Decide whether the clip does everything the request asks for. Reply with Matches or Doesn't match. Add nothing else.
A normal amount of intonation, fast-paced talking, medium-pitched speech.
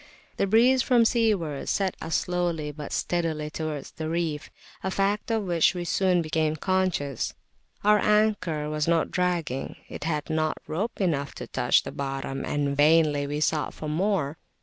Doesn't match